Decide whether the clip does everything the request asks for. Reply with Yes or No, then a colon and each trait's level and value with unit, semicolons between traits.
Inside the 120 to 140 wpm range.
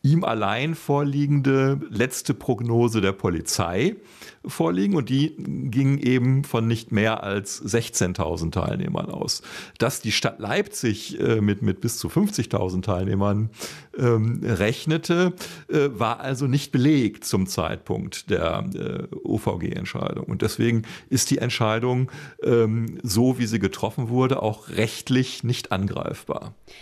Yes: slow, 125 wpm